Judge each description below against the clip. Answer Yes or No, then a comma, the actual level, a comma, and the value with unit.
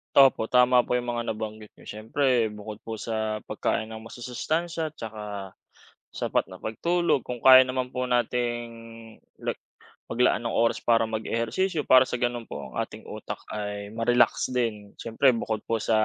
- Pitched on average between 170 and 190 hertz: No, low, 115 Hz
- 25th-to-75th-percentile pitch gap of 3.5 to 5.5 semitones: No, narrow, 2.4 semitones